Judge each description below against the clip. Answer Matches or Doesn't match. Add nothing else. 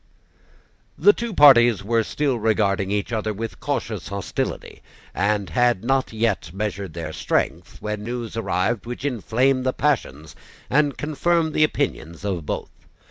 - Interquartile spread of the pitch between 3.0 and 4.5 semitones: Doesn't match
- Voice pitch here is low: Matches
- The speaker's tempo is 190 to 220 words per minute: Doesn't match